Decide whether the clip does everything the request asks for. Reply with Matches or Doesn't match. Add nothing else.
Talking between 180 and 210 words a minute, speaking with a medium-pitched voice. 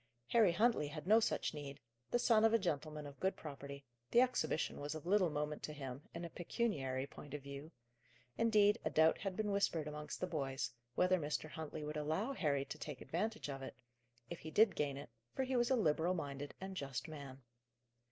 Matches